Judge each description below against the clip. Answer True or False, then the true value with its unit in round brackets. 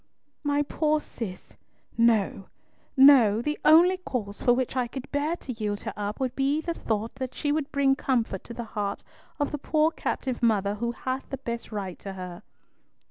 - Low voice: False (250 Hz)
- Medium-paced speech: True (190 wpm)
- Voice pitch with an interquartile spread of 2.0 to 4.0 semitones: False (5.3 semitones)